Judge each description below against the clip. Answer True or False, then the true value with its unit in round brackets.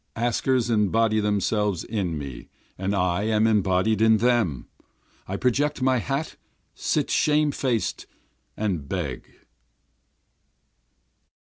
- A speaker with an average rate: False (105 wpm)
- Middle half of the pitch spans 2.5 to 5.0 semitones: True (3.8 semitones)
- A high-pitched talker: False (110 Hz)